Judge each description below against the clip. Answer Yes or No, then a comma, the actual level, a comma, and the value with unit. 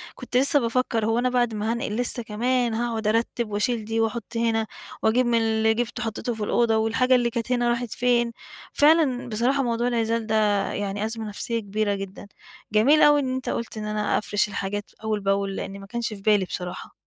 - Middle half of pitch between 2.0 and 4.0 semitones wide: Yes, narrow, 2.4 semitones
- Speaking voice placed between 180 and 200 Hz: No, high, 225 Hz